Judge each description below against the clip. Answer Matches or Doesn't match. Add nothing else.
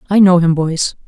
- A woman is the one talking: Matches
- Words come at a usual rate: Doesn't match